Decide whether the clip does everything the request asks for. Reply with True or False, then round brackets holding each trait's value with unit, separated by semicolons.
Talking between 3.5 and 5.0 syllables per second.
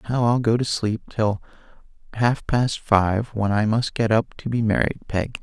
True (4.8 syllables/s)